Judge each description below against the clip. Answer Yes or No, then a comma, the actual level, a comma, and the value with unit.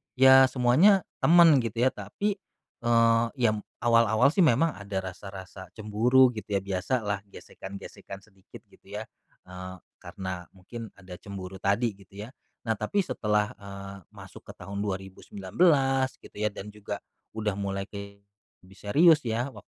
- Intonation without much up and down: No, average, 4.1 semitones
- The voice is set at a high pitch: No, low, 105 Hz